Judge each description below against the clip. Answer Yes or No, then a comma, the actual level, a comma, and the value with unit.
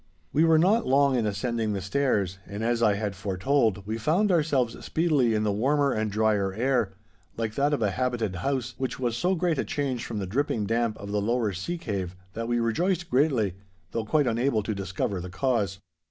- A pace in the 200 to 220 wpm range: Yes, fast, 205 wpm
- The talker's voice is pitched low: Yes, low, 115 Hz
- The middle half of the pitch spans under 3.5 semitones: No, average, 5.1 semitones